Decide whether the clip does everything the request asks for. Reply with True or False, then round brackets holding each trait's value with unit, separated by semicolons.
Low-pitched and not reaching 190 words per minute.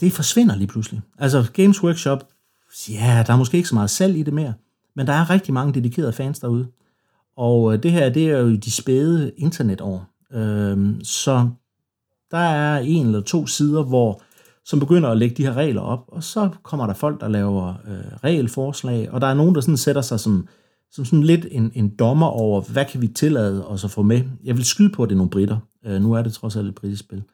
False (125 Hz; 225 wpm)